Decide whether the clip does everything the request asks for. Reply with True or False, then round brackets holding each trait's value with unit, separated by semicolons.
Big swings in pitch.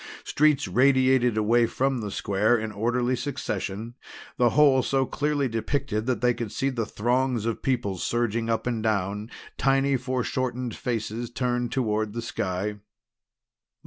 False (3.1 semitones)